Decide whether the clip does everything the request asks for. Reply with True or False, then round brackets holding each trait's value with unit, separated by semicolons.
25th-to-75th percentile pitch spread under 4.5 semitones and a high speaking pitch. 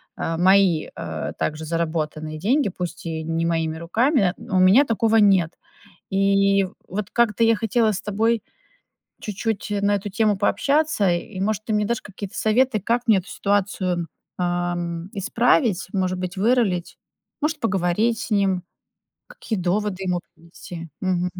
True (3.7 semitones; 195 Hz)